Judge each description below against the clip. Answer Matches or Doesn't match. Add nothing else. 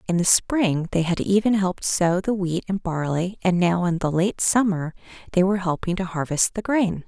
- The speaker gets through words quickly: Matches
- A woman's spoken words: Matches